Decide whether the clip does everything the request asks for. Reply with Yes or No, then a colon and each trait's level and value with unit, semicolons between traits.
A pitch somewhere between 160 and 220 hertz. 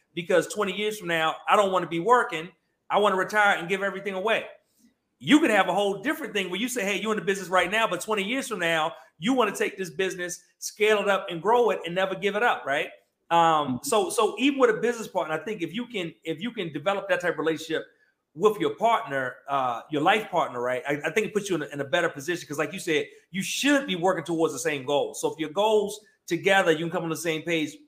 Yes: high, 190 Hz